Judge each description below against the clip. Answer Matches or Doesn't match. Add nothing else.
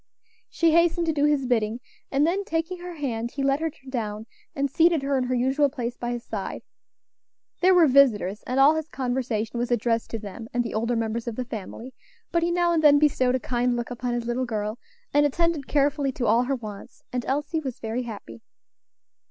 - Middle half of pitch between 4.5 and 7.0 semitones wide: Doesn't match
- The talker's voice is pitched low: Doesn't match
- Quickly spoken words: Matches